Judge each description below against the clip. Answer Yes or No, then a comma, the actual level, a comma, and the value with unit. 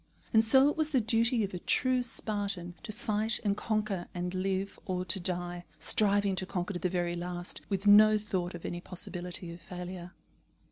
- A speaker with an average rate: Yes, average, 190 wpm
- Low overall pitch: No, high, 190 Hz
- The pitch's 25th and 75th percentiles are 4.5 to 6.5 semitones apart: No, average, 3.2 semitones